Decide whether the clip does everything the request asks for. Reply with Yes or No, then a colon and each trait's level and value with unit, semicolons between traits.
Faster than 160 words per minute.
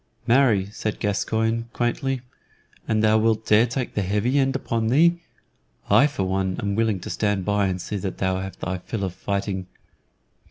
Yes: average, 175 wpm